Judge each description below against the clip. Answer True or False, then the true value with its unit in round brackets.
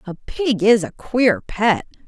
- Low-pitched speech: False (210 Hz)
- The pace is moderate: True (175 wpm)